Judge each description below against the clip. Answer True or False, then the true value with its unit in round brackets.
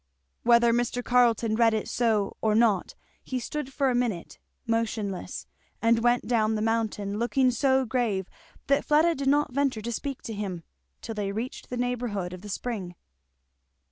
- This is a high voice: True (230 Hz)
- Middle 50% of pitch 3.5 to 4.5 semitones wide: False (2.7 semitones)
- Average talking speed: True (170 wpm)